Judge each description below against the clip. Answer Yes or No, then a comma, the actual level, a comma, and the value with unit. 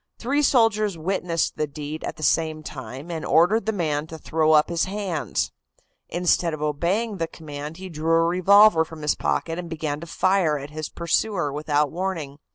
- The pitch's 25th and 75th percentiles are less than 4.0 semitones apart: Yes, average, 3.5 semitones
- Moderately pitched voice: Yes, medium, 165 Hz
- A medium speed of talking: Yes, average, 185 wpm